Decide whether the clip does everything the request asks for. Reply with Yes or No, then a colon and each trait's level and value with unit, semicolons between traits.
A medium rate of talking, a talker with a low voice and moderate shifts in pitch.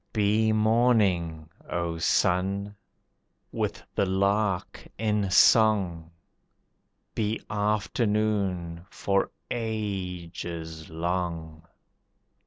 No: slow, 65 wpm; very low, 95 Hz; average, 3.9 semitones